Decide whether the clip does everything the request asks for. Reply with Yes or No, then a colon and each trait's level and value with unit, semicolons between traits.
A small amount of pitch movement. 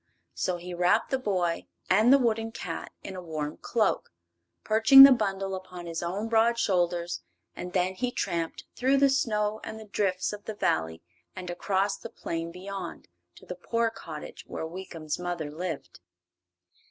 No: average, 4.2 semitones